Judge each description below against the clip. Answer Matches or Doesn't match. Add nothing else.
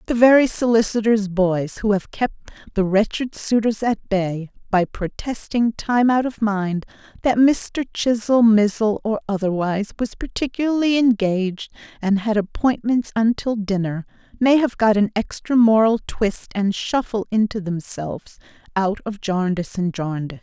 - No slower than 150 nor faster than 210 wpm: Doesn't match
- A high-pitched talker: Matches